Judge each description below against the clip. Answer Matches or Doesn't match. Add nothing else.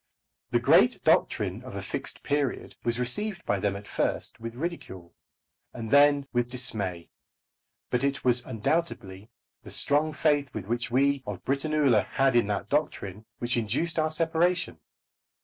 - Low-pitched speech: Matches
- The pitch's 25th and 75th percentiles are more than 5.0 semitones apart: Matches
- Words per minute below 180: Matches